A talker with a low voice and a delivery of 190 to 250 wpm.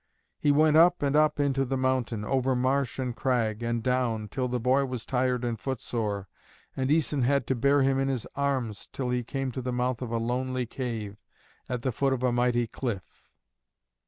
Yes: low, 125 Hz; average, 200 wpm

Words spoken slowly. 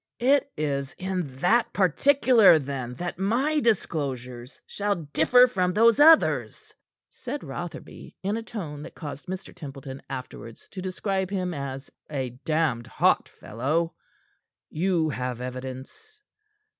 Yes: slow, 125 wpm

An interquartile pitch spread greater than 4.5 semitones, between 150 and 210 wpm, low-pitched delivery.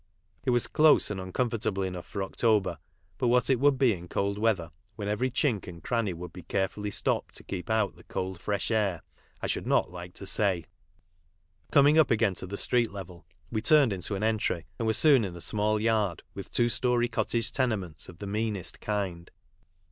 No: average, 4.0 semitones; average, 200 wpm; low, 105 Hz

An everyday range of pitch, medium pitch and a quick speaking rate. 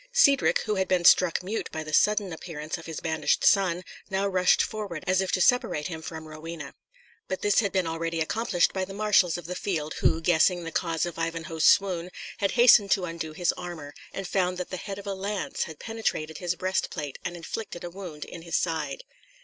Yes: average, 3.1 semitones; medium, 175 Hz; fast, 215 wpm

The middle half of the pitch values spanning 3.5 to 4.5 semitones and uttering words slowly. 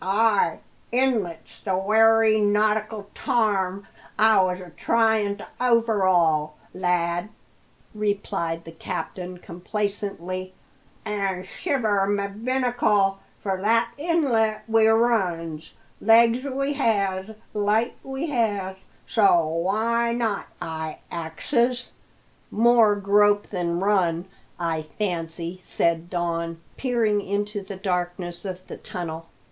Yes: average, 3.9 semitones; slow, 105 wpm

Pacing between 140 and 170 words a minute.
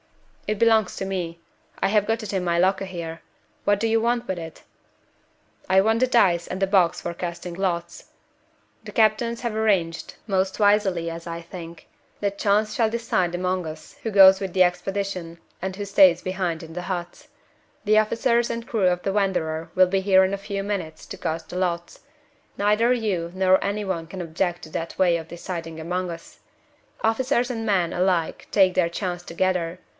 No: average, 190 wpm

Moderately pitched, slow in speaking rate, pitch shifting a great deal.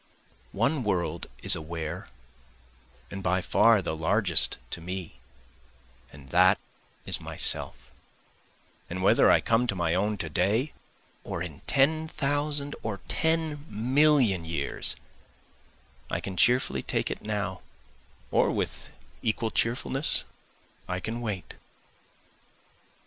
No: low, 100 Hz; slow, 115 wpm; wide, 6.5 semitones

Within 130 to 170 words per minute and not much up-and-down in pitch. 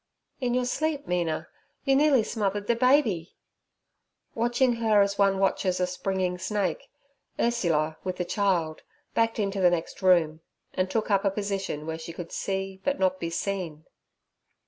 No: average, 160 wpm; average, 4.1 semitones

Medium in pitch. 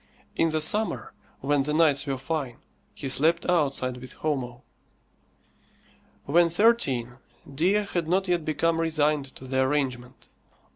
Yes: medium, 150 Hz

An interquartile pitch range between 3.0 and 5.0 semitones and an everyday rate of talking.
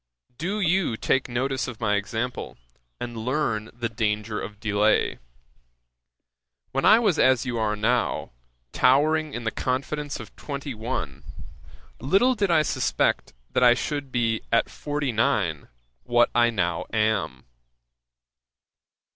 No: average, 4.5 semitones; slow, 130 wpm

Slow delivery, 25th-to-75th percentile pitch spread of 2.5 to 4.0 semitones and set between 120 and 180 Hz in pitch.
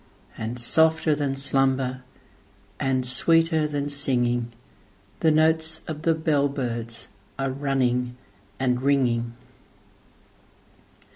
Yes: slow, 90 wpm; average, 3.6 semitones; low, 135 Hz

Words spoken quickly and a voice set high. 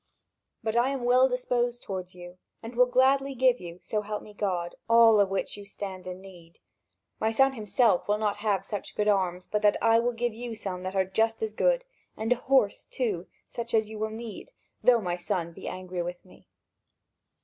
Yes: fast, 210 wpm; high, 215 Hz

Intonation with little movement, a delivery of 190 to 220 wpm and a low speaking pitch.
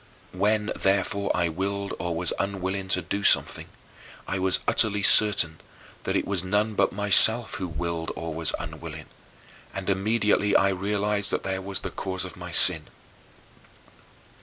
No: narrow, 2.1 semitones; average, 155 wpm; very low, 95 Hz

